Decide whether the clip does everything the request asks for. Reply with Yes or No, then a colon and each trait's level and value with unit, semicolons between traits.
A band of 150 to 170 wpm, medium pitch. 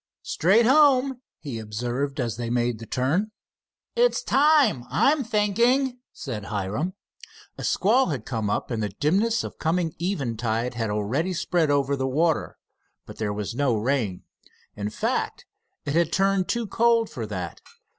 Yes: average, 155 wpm; medium, 145 Hz